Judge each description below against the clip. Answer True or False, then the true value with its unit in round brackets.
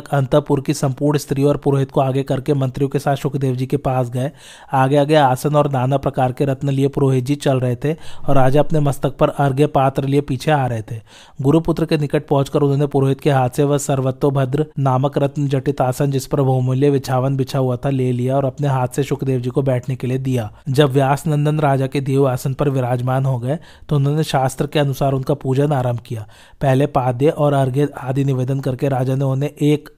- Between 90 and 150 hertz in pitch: True (140 Hz)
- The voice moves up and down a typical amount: False (1.8 semitones)